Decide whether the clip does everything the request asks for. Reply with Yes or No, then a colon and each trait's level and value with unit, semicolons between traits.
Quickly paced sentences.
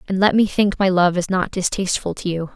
Yes: fast, 260 wpm